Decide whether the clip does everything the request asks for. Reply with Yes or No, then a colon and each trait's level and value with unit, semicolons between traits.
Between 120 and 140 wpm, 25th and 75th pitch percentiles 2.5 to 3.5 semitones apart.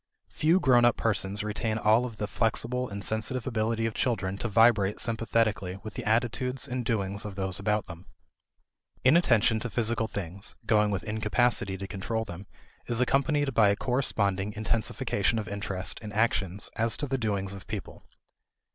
No: average, 165 wpm; average, 3.0 semitones